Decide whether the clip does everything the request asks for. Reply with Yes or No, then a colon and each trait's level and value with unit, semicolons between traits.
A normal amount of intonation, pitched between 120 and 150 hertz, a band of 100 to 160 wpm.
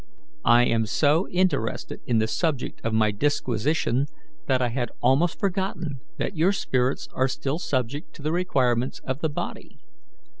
Yes: average, 4.8 semitones; low, 135 Hz; average, 155 wpm